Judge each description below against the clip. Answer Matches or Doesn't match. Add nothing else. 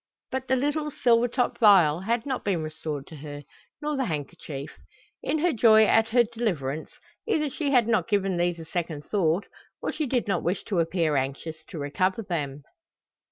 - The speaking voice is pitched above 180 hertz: Matches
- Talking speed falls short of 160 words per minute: Doesn't match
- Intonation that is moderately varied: Doesn't match